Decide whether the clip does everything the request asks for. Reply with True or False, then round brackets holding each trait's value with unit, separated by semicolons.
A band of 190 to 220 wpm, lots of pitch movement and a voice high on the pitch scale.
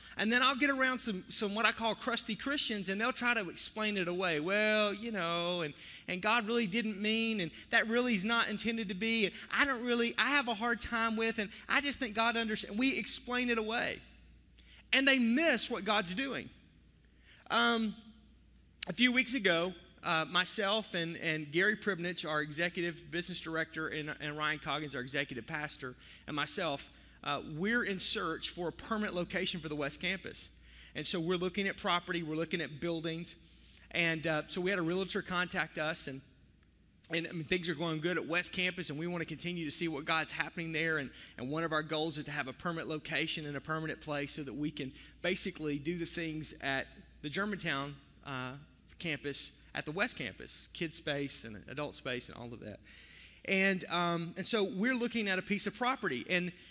False (205 wpm; 5.8 semitones; 175 Hz)